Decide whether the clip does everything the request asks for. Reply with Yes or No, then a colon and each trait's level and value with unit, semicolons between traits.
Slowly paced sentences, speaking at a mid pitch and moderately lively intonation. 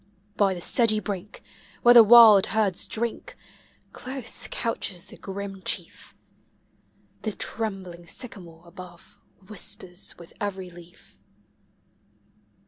No: slow, 105 wpm; high, 195 Hz; average, 3.6 semitones